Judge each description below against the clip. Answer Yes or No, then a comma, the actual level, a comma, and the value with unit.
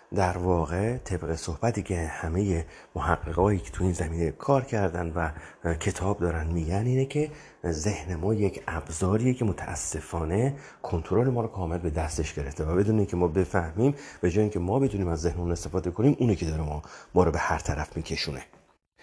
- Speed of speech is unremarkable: No, fast, 175 wpm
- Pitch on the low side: Yes, very low, 90 Hz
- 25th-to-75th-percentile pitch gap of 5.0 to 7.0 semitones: No, average, 4.1 semitones